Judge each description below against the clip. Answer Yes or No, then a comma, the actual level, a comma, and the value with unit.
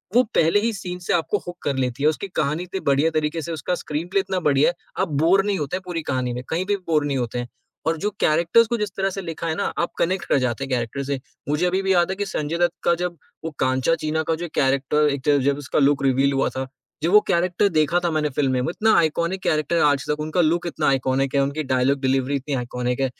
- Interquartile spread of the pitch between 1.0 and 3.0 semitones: No, average, 4.3 semitones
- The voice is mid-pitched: Yes, medium, 155 Hz